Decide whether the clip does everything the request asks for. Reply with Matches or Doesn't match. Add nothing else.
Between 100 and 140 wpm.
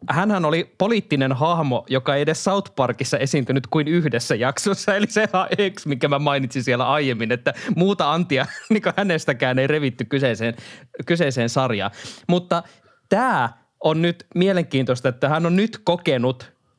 Doesn't match